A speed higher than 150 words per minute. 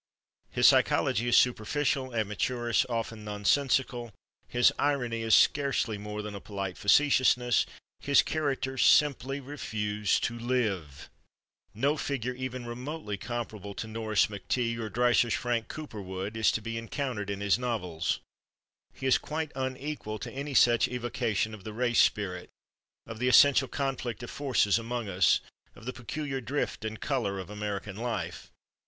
No: average, 145 wpm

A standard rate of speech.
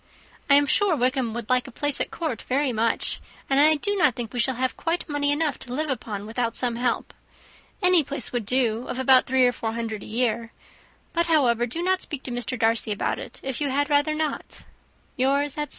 No: fast, 220 wpm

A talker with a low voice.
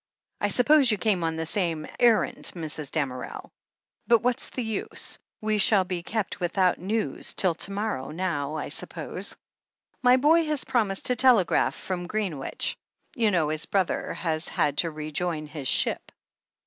No: medium, 185 Hz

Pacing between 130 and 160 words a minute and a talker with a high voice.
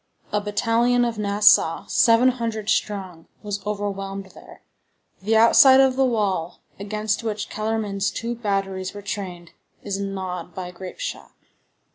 Yes: slow, 135 wpm; high, 205 Hz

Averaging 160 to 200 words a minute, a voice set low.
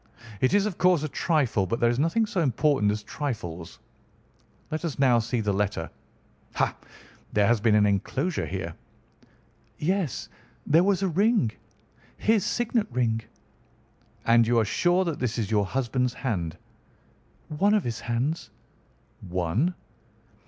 No: average, 145 wpm; low, 125 Hz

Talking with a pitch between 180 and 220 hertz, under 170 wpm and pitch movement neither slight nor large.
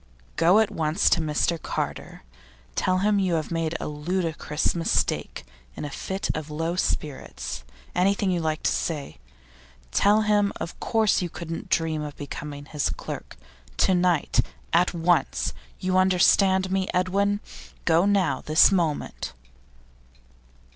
No: medium, 170 Hz; average, 140 wpm; average, 3.5 semitones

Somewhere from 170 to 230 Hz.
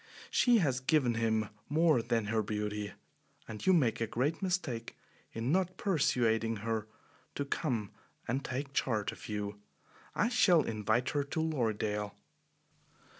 No: low, 120 Hz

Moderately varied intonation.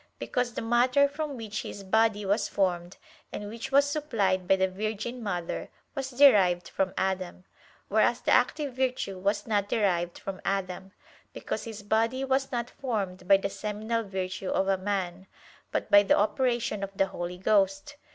Yes: average, 4.0 semitones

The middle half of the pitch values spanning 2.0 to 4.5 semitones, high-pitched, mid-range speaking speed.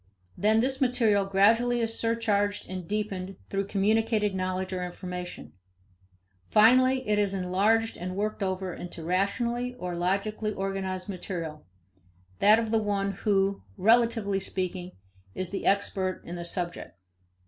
No: average, 3.0 semitones; high, 200 Hz; slow, 130 wpm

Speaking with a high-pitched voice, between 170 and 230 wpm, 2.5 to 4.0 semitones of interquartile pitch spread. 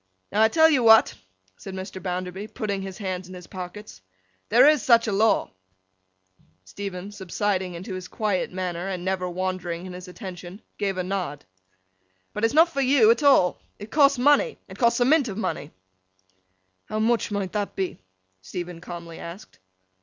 Yes: high, 195 Hz; average, 175 wpm; average, 3.7 semitones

